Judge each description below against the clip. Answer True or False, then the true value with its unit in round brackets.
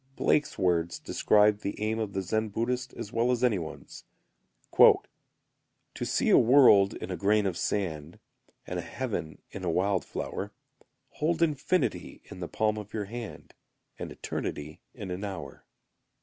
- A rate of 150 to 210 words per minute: True (160 wpm)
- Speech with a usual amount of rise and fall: True (4.1 semitones)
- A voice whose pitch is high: False (105 Hz)